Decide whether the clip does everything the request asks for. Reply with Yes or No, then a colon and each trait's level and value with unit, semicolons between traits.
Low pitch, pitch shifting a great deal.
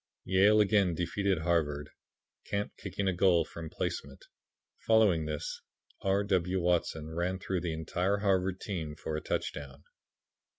No: very low, 90 Hz; average, 3.4 semitones